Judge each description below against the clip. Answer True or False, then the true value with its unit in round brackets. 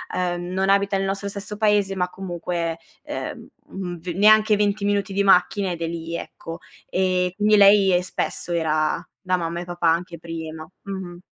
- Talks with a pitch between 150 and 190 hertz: True (185 Hz)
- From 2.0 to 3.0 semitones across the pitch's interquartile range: True (2.7 semitones)